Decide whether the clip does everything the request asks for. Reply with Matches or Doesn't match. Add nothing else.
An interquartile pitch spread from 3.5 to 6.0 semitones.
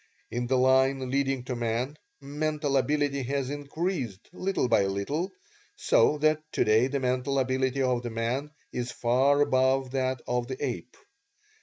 Doesn't match